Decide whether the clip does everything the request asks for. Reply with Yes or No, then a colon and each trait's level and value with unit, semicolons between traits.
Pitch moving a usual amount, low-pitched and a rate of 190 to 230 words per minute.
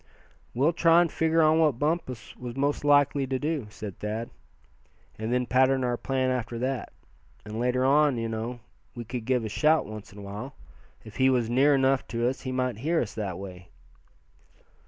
Yes: average, 3.8 semitones; low, 125 Hz; average, 195 wpm